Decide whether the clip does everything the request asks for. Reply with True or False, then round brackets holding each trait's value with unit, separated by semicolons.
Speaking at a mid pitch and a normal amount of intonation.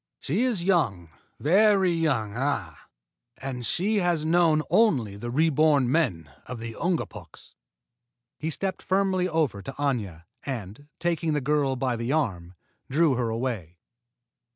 False (145 Hz; 6.4 semitones)